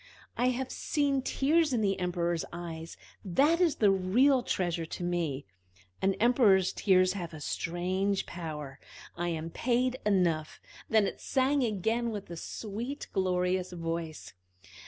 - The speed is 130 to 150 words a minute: Yes, average, 140 wpm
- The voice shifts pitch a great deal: Yes, wide, 5.9 semitones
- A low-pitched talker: No, high, 190 Hz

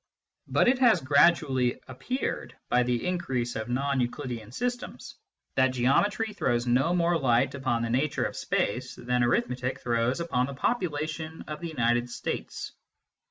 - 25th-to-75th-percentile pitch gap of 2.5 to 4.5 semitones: No, average, 5.2 semitones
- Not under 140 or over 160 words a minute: Yes, average, 155 wpm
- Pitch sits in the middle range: No, low, 130 Hz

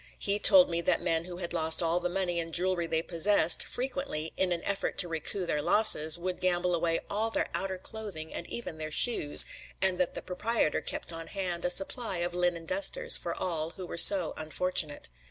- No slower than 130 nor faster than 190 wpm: No, fast, 205 wpm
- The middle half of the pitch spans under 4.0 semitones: Yes, average, 2.7 semitones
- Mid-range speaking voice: Yes, medium, 175 Hz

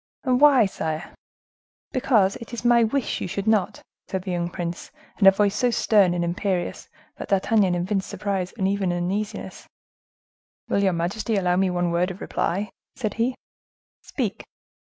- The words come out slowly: No, average, 165 wpm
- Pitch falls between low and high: No, high, 195 Hz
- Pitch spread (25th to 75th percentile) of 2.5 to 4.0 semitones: Yes, average, 3.6 semitones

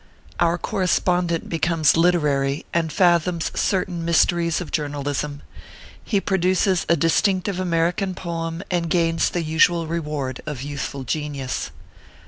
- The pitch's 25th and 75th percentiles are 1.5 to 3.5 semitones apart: Yes, average, 2.8 semitones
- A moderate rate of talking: No, slow, 120 wpm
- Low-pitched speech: No, medium, 165 Hz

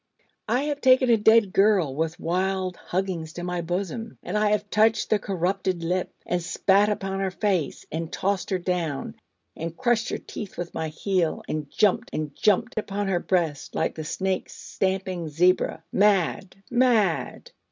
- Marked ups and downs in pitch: No, average, 3.5 semitones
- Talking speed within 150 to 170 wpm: Yes, average, 165 wpm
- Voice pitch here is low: No, high, 190 Hz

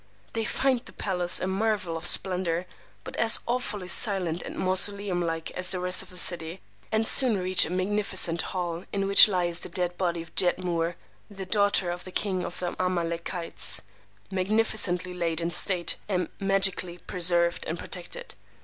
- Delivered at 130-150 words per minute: No, average, 165 wpm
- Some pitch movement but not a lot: No, narrow, 2.3 semitones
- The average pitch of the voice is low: No, medium, 185 Hz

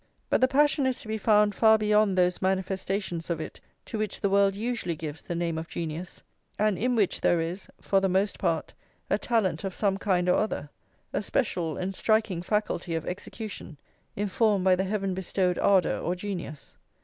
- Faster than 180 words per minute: Yes, average, 190 wpm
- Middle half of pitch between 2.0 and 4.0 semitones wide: Yes, average, 3.2 semitones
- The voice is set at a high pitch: Yes, high, 195 Hz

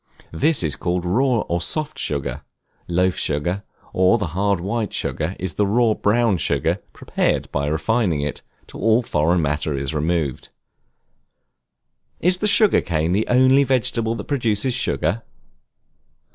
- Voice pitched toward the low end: Yes, very low, 95 Hz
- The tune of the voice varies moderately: No, wide, 6.6 semitones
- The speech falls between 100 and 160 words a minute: Yes, average, 145 wpm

